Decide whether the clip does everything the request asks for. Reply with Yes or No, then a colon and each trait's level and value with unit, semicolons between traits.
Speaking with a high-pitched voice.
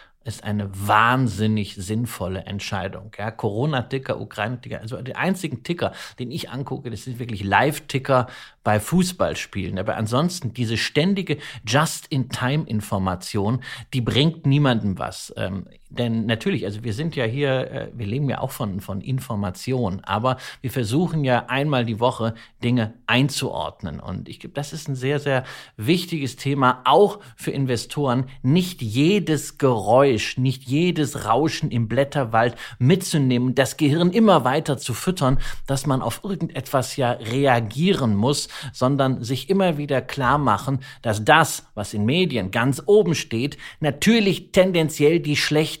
No: low, 130 Hz